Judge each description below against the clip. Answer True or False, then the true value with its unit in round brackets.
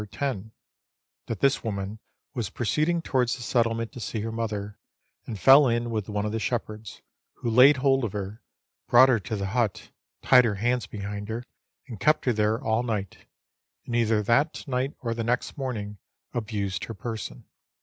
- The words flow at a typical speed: True (180 wpm)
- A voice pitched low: True (115 Hz)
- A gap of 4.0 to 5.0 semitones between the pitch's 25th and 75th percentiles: False (3.0 semitones)